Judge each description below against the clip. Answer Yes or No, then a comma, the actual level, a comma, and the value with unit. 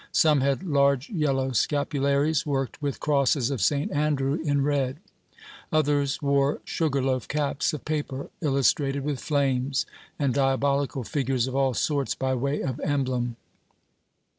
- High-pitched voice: No, medium, 140 Hz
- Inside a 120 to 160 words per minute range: Yes, average, 140 wpm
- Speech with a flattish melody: Yes, narrow, 1.6 semitones